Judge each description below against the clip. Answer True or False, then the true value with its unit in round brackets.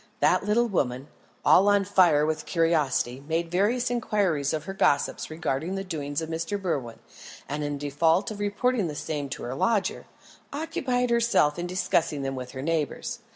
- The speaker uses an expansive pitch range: True (5.8 semitones)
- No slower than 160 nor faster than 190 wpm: True (170 wpm)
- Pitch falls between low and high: True (165 Hz)